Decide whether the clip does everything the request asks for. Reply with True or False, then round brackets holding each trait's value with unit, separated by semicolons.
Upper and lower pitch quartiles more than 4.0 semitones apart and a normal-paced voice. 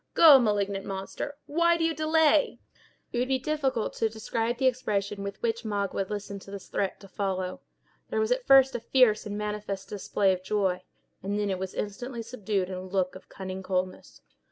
True (4.8 semitones; 190 wpm)